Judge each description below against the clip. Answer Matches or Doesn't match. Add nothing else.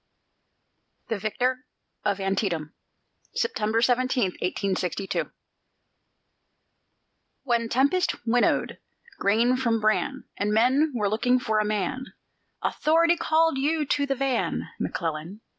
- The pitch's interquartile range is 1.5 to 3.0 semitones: Doesn't match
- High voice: Matches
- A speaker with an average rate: Doesn't match